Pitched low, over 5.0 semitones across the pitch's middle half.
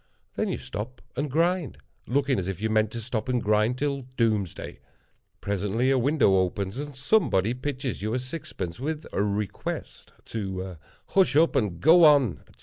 Yes: low, 120 Hz; wide, 5.6 semitones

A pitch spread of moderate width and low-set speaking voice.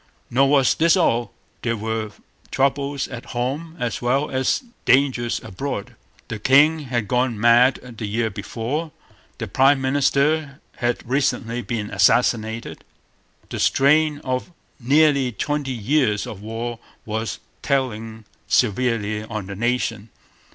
Yes: average, 3.6 semitones; low, 125 Hz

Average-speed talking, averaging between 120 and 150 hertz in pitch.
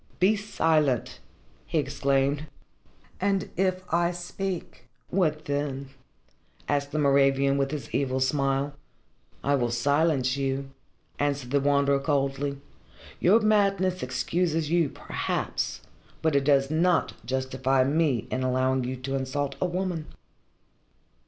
No: slow, 120 wpm; medium, 140 Hz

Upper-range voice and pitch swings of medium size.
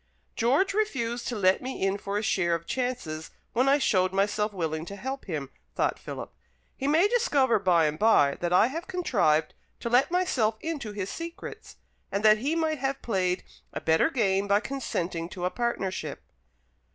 No: high, 215 Hz; wide, 6.6 semitones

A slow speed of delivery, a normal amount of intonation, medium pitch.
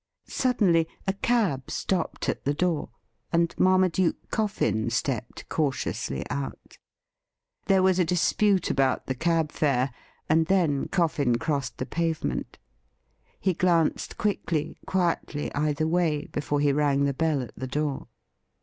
Yes: slow, 130 wpm; average, 4.4 semitones; medium, 155 Hz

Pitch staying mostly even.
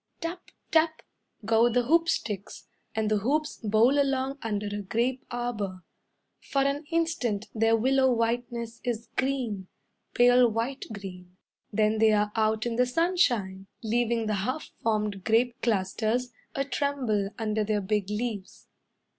No: average, 3.5 semitones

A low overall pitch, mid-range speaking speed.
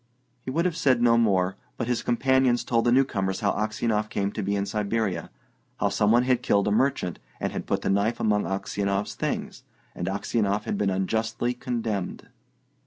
Yes: low, 110 Hz; average, 185 wpm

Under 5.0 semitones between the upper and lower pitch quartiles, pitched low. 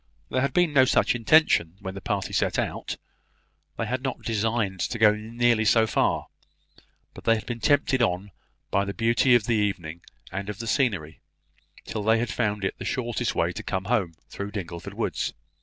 Yes: average, 3.4 semitones; low, 110 Hz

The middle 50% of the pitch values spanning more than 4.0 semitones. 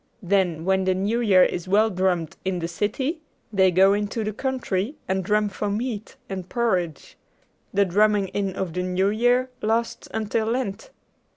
No: average, 3.0 semitones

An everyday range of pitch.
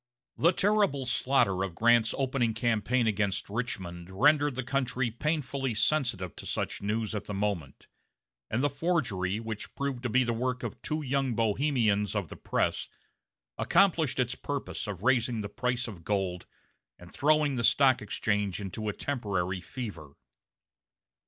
Yes: average, 4.8 semitones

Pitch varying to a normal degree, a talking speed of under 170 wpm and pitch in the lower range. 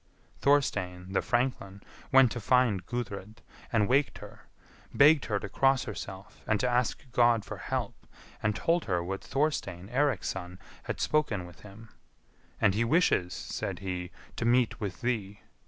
Yes: average, 4.7 semitones; average, 155 wpm; low, 110 Hz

